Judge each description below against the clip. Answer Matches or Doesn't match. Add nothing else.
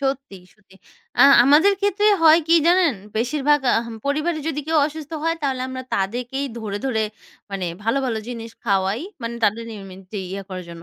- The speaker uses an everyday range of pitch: Doesn't match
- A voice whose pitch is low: Doesn't match